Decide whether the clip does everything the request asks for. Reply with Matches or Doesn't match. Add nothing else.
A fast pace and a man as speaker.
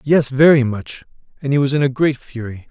Matches